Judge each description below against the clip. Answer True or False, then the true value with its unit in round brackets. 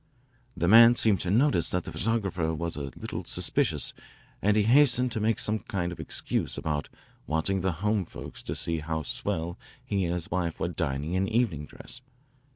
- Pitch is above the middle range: False (90 Hz)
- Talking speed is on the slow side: False (185 wpm)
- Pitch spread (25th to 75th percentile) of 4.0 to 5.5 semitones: True (4.9 semitones)